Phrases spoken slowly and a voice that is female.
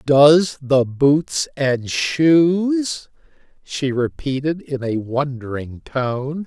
No: slow, 100 wpm; male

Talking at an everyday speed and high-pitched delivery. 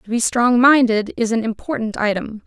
Yes: average, 195 wpm; high, 230 Hz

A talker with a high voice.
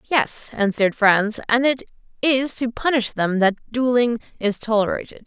Yes: high, 230 Hz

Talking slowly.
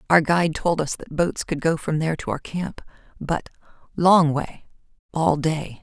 No: average, 165 wpm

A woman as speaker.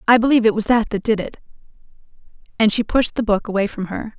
Yes: female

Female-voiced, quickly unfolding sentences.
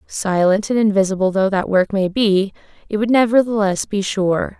No: female; average, 170 wpm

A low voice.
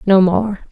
No: high, 195 Hz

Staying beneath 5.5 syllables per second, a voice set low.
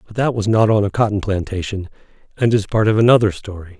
No: 6.3 syllables/s; low, 105 Hz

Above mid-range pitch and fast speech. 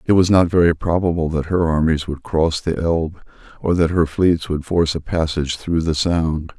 No: very low, 80 Hz; fast, 210 wpm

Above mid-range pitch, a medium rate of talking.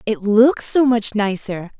Yes: high, 220 Hz; average, 170 wpm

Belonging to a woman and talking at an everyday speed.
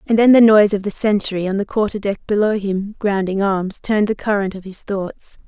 No: female; fast, 230 wpm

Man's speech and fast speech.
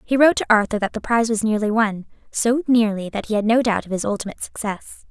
No: female; fast, 245 wpm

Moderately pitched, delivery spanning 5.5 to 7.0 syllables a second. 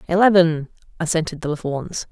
Yes: medium, 165 Hz; 6.3 syllables/s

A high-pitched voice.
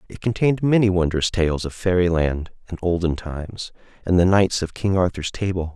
No: very low, 90 Hz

